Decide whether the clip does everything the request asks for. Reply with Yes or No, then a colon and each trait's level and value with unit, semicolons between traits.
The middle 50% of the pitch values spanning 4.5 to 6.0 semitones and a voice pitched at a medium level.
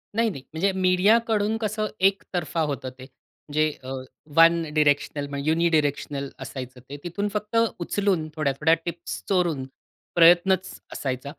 Yes: average, 5.2 semitones; medium, 170 Hz